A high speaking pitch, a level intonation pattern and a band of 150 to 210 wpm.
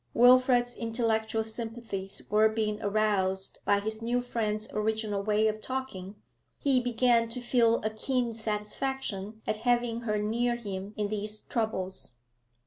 No: high, 220 Hz; narrow, 2.2 semitones; slow, 135 wpm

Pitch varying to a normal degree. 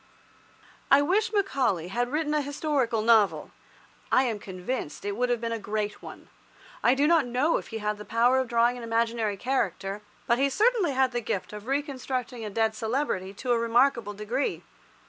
Yes: average, 4.0 semitones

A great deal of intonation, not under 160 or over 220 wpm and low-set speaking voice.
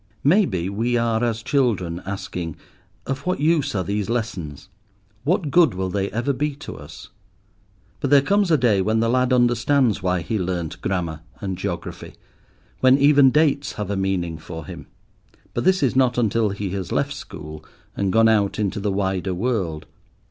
Yes: wide, 5.9 semitones; average, 175 wpm; low, 110 Hz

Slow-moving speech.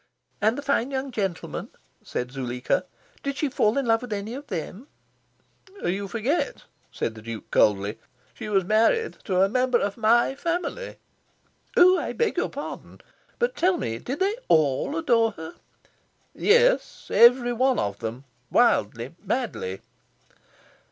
No: average, 145 wpm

